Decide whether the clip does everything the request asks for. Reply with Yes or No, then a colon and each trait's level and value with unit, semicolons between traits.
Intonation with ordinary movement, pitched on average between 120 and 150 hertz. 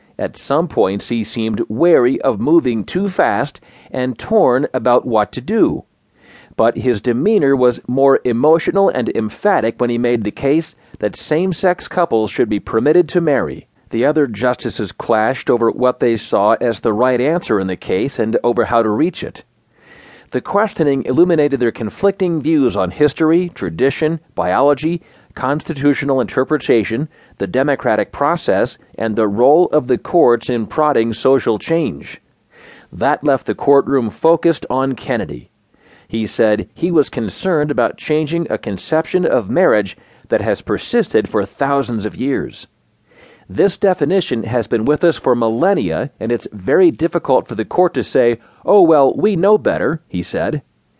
No: wide, 6.1 semitones; low, 135 Hz